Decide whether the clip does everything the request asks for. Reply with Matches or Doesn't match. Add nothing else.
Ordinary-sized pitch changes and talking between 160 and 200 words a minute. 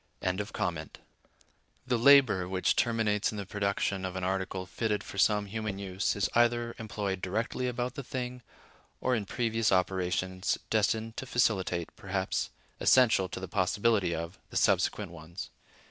Doesn't match